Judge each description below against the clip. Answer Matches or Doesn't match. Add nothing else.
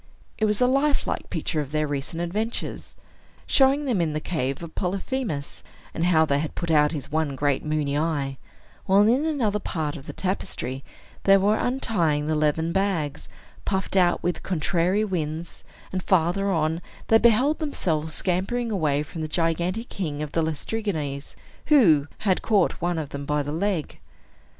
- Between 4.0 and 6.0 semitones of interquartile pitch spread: Matches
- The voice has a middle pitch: Matches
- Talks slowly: Doesn't match